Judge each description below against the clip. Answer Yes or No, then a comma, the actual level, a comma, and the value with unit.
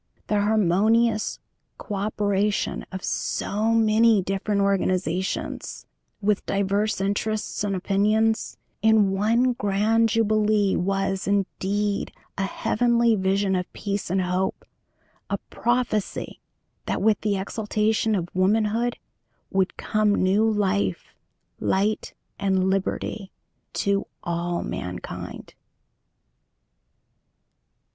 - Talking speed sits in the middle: No, slow, 95 wpm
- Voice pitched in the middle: No, high, 205 Hz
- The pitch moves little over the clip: Yes, narrow, 2.0 semitones